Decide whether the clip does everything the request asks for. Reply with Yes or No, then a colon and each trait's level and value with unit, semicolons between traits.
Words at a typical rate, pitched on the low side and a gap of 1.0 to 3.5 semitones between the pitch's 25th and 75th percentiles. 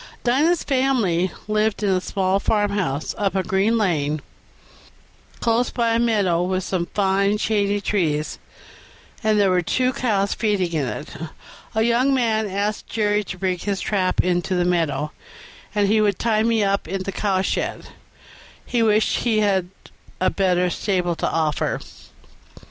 No: average, 150 wpm; high, 200 Hz; average, 3.1 semitones